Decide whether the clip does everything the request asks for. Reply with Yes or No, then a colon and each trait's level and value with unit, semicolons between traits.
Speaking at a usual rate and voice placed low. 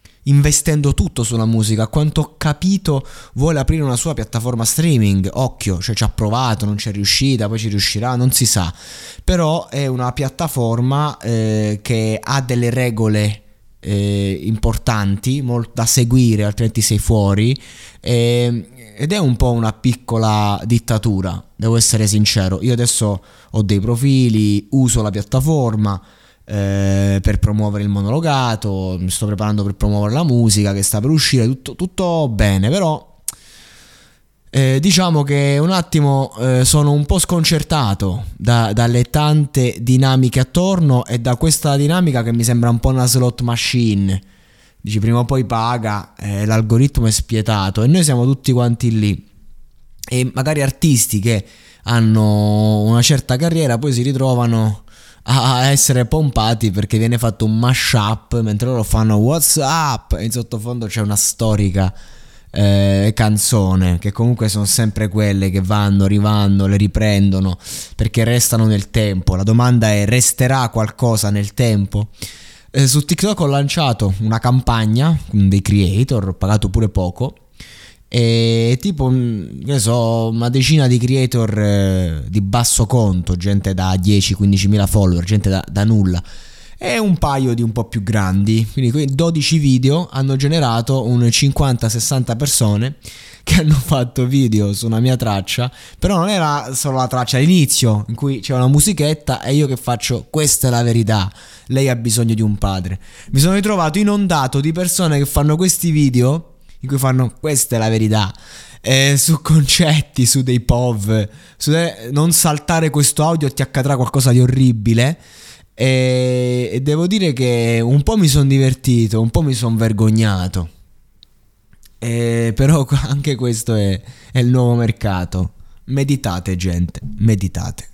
Yes: average, 150 wpm; low, 120 Hz